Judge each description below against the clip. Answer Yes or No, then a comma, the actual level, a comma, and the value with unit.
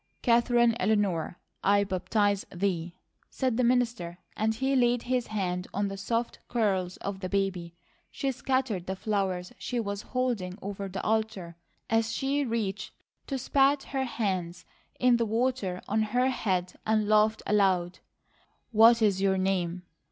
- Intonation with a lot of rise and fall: No, average, 4.1 semitones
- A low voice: No, high, 210 Hz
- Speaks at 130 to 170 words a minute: Yes, average, 150 wpm